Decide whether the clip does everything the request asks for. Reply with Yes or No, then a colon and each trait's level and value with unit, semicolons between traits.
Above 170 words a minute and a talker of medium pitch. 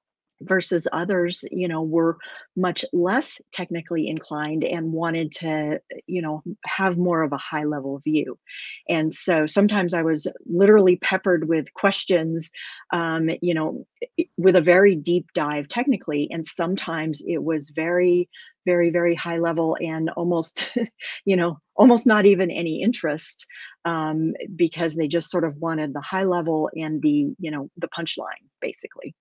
No: average, 150 wpm; medium, 170 Hz